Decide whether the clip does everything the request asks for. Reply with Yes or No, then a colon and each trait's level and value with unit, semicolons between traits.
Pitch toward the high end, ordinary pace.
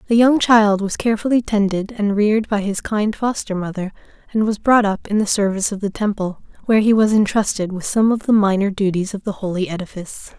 No: high, 205 Hz; fast, 215 wpm